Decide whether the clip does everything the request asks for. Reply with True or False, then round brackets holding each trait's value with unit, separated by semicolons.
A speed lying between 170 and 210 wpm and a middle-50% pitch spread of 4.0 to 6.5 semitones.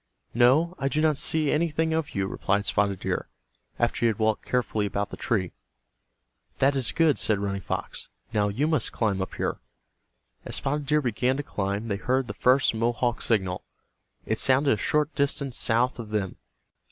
True (180 wpm; 5.5 semitones)